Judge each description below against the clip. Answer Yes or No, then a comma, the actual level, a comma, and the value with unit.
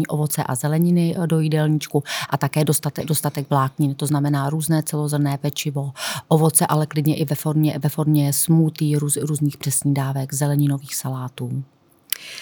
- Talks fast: No, average, 140 wpm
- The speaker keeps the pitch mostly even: Yes, narrow, 1.5 semitones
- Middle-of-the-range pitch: Yes, medium, 150 Hz